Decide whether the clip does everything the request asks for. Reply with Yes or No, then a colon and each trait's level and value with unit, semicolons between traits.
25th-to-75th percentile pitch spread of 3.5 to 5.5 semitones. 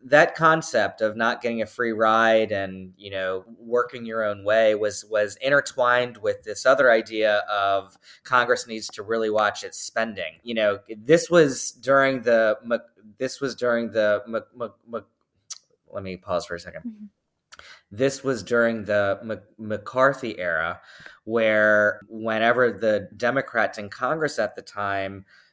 No: average, 2.9 semitones